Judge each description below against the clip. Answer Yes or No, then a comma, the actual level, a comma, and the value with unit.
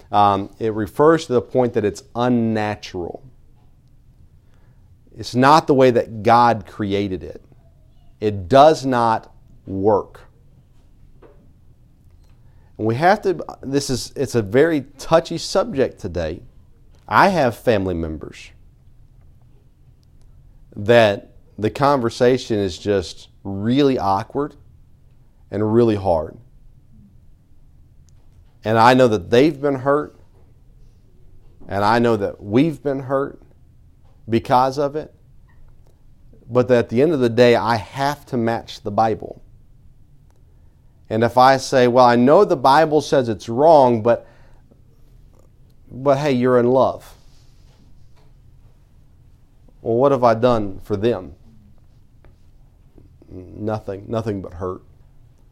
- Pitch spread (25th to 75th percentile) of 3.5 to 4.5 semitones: Yes, average, 4.0 semitones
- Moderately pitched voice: No, low, 115 Hz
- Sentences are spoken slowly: Yes, slow, 115 wpm